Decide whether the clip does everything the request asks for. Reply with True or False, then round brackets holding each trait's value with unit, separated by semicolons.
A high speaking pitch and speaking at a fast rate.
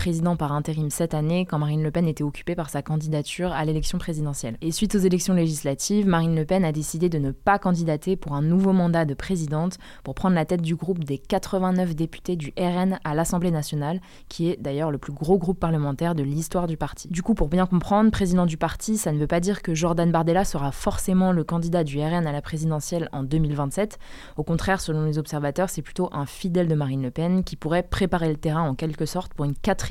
False (165 Hz; 230 wpm)